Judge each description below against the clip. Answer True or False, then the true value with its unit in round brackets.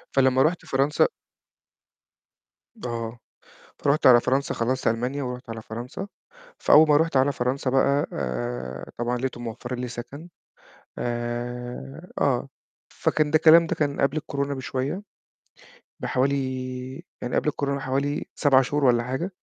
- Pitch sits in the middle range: False (130 Hz)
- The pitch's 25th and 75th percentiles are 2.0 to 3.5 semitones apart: True (3.0 semitones)